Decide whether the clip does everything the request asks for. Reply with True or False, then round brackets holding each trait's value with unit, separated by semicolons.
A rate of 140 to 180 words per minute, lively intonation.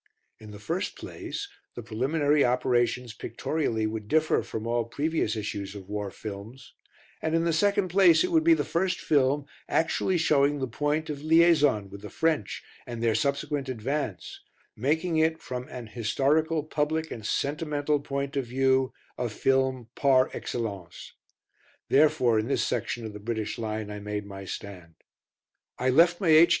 True (160 wpm; 6.0 semitones)